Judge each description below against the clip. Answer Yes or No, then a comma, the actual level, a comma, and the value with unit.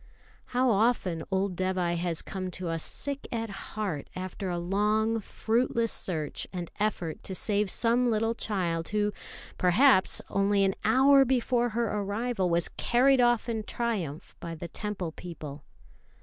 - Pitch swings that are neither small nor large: Yes, average, 4.5 semitones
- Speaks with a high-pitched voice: Yes, high, 205 Hz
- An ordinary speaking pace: Yes, average, 150 wpm